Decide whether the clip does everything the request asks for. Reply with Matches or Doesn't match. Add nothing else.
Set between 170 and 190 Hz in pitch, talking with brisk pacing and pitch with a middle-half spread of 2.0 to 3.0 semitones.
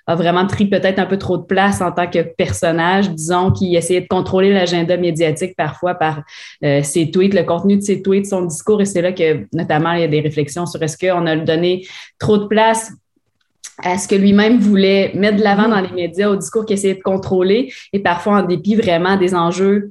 Matches